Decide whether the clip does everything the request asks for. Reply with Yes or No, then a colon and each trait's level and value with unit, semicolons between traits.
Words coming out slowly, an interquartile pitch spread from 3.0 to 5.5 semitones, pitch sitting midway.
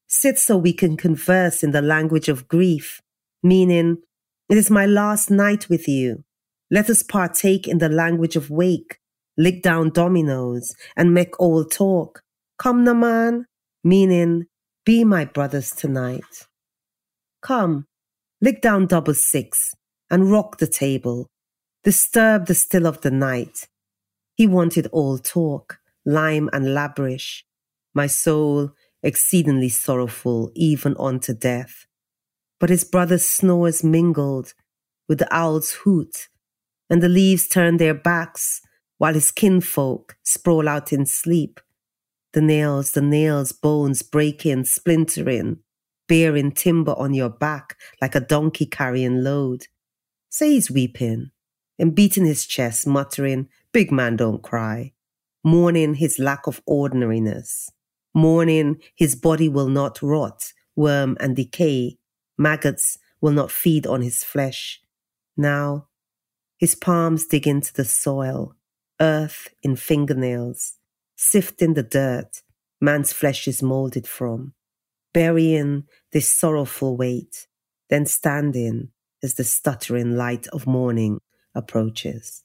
Yes: slow, 125 wpm; average, 4.4 semitones; medium, 150 Hz